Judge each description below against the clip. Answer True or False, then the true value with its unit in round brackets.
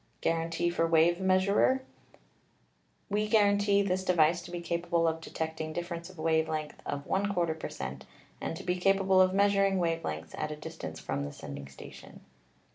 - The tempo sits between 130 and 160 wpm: False (175 wpm)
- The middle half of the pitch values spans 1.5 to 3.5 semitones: True (3.1 semitones)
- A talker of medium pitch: True (170 Hz)